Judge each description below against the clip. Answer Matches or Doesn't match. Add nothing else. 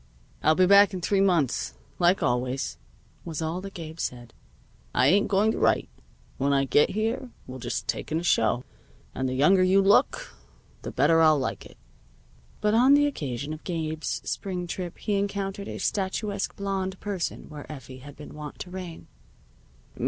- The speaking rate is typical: Matches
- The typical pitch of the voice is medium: Matches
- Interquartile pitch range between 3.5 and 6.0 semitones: Matches